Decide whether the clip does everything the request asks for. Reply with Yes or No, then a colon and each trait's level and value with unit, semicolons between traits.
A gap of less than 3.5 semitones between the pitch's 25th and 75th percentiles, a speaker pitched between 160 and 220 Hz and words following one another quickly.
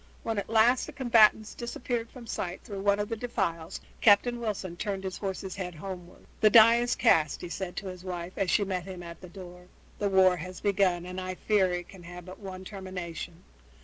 Yes: average, 3.0 semitones; high, 190 Hz; fast, 215 wpm